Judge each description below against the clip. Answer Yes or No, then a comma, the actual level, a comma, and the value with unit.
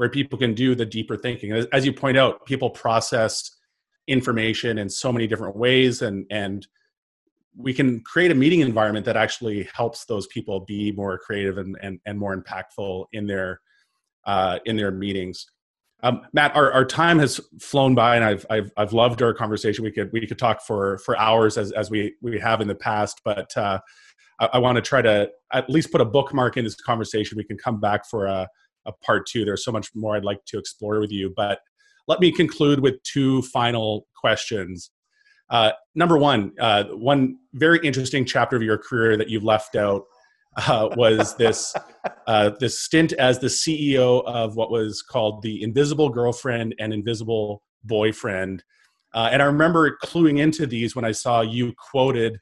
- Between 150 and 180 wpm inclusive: No, average, 190 wpm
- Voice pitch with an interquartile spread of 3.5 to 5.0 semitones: Yes, average, 4.0 semitones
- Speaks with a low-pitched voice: Yes, low, 115 Hz